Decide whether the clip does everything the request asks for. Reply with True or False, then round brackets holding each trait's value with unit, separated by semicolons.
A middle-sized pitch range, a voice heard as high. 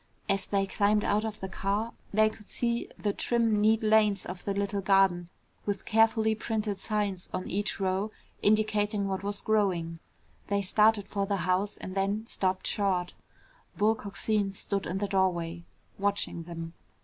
False (1.9 semitones; 200 Hz)